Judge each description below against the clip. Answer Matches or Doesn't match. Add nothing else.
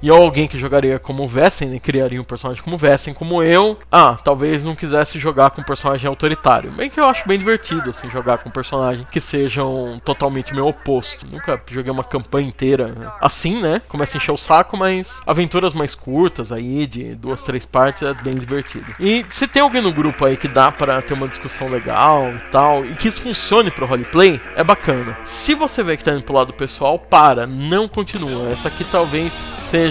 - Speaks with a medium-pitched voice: Matches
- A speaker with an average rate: Doesn't match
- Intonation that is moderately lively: Matches